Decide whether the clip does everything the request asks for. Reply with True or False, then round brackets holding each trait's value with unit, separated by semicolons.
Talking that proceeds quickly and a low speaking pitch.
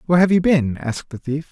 False (275 wpm; 150 Hz)